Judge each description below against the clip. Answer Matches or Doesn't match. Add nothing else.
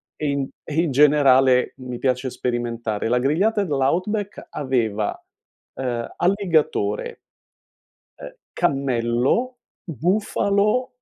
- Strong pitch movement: Matches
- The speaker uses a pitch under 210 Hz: Matches